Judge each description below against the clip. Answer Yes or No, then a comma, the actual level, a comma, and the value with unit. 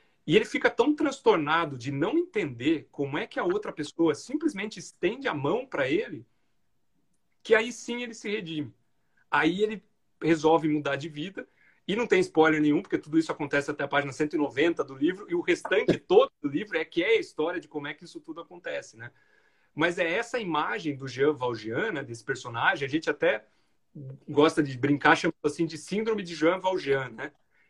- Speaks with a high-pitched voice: No, medium, 160 Hz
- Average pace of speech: No, fast, 195 wpm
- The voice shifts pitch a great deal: Yes, wide, 7.6 semitones